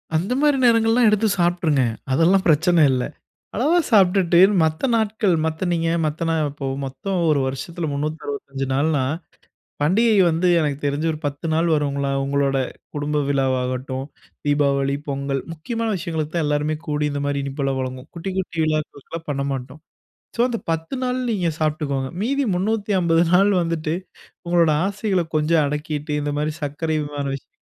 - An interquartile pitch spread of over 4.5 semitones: No, average, 3.9 semitones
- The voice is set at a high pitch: No, medium, 155 Hz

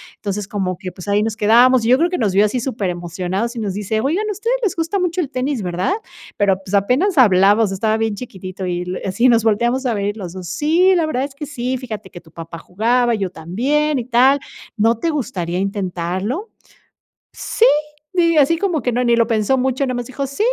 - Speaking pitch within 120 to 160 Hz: No, high, 230 Hz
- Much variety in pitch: Yes, wide, 5.8 semitones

